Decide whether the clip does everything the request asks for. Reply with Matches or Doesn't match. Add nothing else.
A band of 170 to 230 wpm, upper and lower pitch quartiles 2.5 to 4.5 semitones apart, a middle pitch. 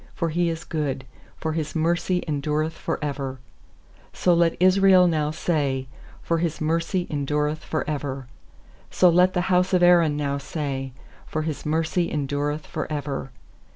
Doesn't match